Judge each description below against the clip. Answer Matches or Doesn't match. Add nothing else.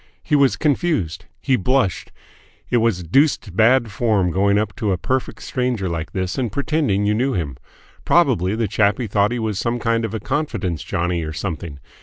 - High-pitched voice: Doesn't match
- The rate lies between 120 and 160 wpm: Doesn't match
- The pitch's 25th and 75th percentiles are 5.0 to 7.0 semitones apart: Matches